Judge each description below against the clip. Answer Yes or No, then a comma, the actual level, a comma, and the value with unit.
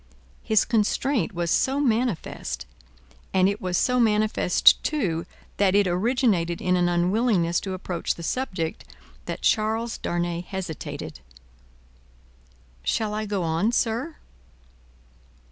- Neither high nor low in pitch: No, high, 200 Hz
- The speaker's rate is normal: No, slow, 115 wpm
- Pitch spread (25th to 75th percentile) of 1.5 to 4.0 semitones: No, average, 4.6 semitones